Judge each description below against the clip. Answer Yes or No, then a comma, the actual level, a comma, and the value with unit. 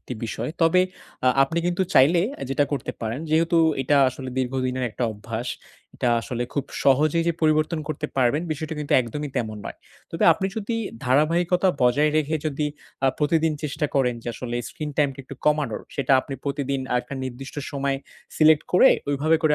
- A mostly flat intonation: No, average, 3.3 semitones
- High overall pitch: No, medium, 145 Hz